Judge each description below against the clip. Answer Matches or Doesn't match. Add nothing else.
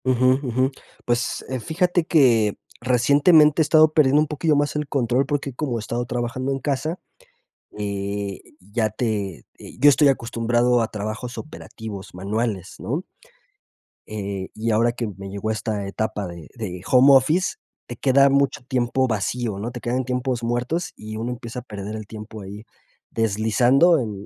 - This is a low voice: Matches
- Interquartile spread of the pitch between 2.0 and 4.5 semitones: Matches